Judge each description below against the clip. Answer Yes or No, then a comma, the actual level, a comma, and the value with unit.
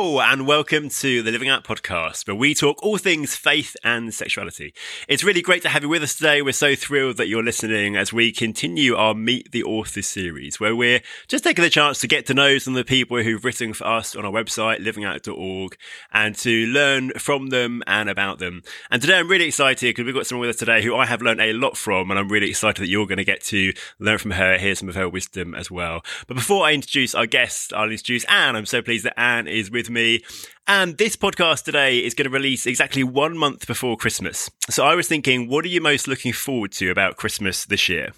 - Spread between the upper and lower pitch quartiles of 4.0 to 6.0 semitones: Yes, average, 5.0 semitones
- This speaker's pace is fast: Yes, fast, 240 wpm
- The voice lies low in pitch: Yes, low, 120 Hz